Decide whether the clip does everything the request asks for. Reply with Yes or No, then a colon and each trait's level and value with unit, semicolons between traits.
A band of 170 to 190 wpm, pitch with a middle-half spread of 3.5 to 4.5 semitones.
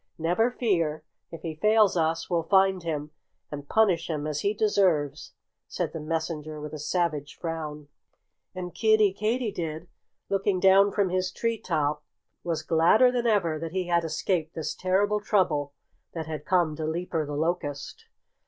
No: average, 160 wpm; average, 4.1 semitones